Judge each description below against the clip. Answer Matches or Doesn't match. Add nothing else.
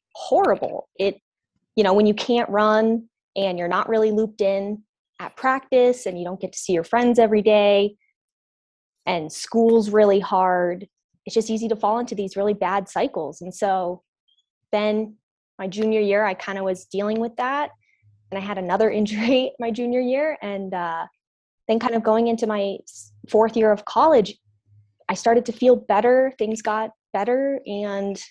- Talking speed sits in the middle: Matches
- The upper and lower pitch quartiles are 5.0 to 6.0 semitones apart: Doesn't match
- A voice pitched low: Doesn't match